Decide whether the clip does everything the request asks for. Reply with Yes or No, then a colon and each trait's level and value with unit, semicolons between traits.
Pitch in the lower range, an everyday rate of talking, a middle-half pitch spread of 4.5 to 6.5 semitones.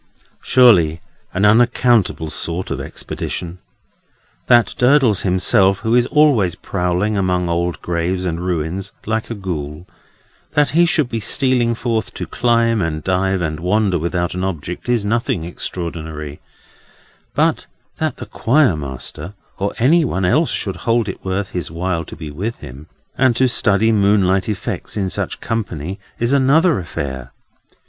Yes: very low, 95 Hz; average, 145 wpm; average, 5.3 semitones